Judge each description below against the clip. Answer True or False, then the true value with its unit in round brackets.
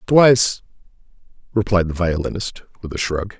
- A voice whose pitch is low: True (95 Hz)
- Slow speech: True (125 wpm)